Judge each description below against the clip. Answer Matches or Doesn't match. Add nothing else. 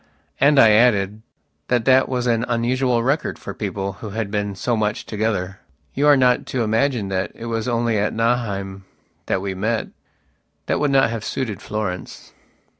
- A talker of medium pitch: Doesn't match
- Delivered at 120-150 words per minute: Doesn't match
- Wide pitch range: Doesn't match